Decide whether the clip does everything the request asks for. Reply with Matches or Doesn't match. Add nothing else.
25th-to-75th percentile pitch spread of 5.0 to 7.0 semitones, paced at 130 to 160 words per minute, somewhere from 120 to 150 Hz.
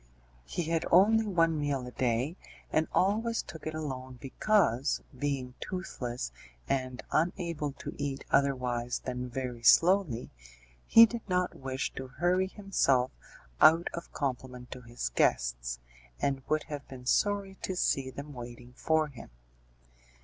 Matches